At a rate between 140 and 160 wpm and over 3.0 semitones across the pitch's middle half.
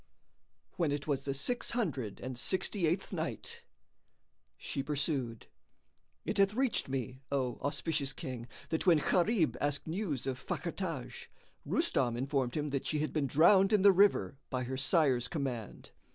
Yes: average, 155 wpm; average, 5.1 semitones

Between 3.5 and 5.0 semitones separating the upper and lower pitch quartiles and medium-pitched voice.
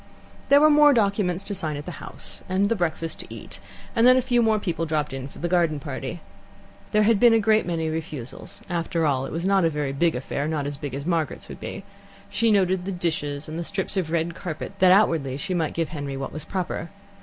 Yes: average, 4.6 semitones; medium, 170 Hz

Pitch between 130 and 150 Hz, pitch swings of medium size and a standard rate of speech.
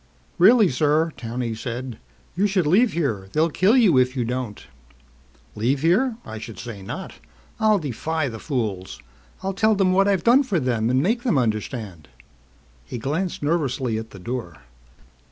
No: low, 135 Hz; wide, 8.5 semitones; average, 165 wpm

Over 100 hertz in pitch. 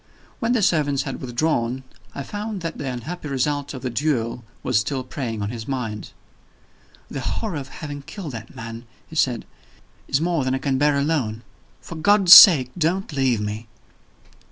Yes: low, 135 Hz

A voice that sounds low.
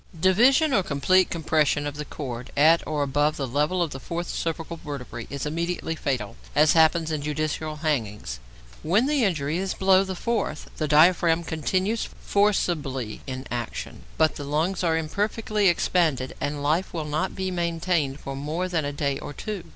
No: medium, 160 Hz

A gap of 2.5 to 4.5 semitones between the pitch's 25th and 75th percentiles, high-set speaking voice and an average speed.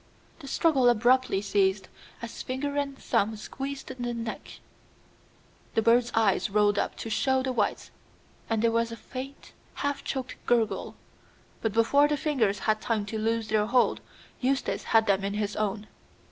Yes: average, 3.6 semitones; high, 230 Hz; average, 160 wpm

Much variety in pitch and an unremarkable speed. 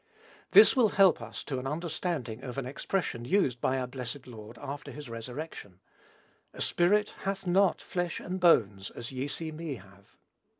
Yes: wide, 6.7 semitones; average, 170 wpm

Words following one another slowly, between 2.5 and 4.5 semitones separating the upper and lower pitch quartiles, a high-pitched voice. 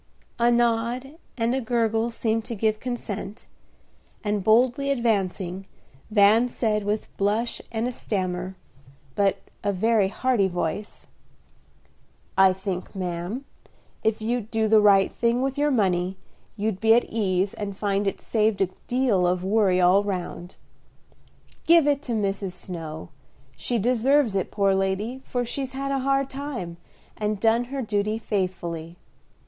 No: average, 145 wpm; average, 3.9 semitones; high, 215 Hz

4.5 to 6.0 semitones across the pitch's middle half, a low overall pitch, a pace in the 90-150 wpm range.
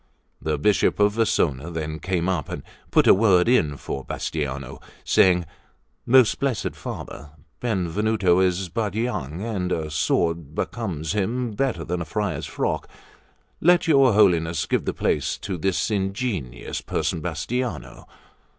Yes: wide, 5.5 semitones; very low, 90 Hz; average, 140 wpm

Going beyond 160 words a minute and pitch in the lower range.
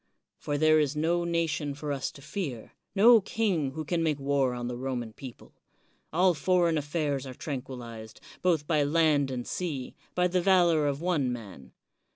No: average, 180 wpm; medium, 150 Hz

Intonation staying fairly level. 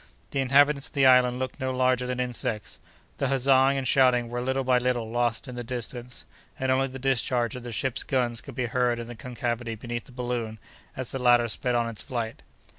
Yes: narrow, 1.6 semitones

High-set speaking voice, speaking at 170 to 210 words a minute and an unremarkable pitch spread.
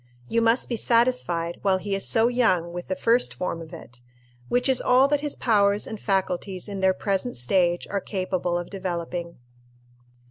Yes: high, 195 Hz; average, 180 wpm; average, 4.7 semitones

